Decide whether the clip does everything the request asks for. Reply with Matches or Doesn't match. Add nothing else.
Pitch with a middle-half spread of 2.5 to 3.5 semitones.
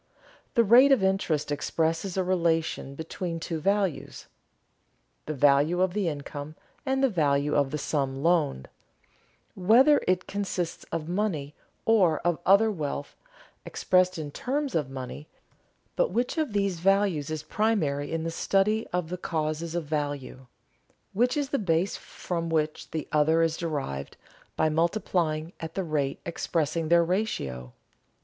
Doesn't match